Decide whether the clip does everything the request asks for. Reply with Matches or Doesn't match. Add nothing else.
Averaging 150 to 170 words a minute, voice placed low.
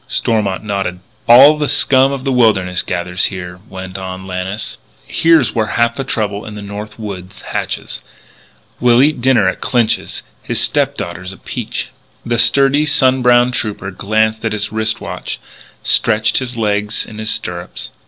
Matches